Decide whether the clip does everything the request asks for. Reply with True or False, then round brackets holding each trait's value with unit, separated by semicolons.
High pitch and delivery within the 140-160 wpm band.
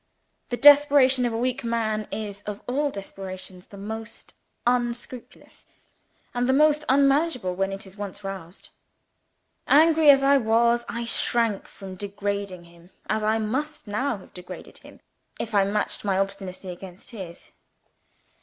True (220 Hz; 145 wpm)